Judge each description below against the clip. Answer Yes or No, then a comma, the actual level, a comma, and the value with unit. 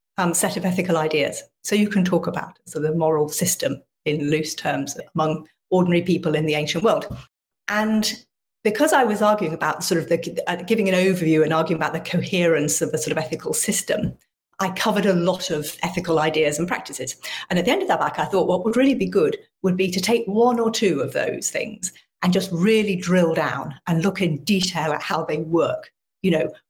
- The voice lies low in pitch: No, medium, 180 Hz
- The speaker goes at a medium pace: No, fast, 215 wpm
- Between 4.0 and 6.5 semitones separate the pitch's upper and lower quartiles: Yes, average, 4.5 semitones